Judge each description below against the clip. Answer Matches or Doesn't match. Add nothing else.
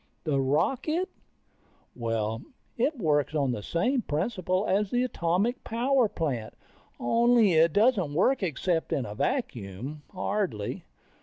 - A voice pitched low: Doesn't match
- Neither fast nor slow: Doesn't match